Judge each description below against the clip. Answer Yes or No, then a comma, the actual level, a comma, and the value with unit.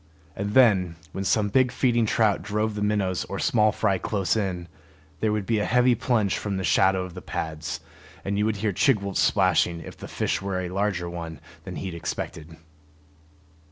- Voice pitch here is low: Yes, low, 100 Hz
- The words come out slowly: No, average, 190 wpm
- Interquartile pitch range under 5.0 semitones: Yes, average, 2.8 semitones